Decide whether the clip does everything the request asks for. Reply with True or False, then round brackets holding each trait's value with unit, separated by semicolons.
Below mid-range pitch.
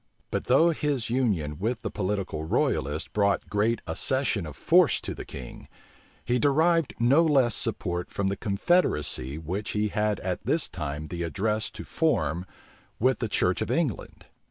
True (105 Hz)